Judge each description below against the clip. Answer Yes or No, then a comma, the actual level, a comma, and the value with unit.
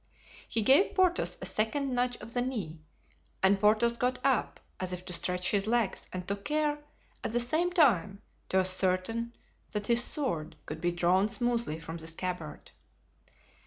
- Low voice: No, high, 210 Hz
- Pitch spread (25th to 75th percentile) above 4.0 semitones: Yes, average, 5.2 semitones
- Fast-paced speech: No, average, 165 wpm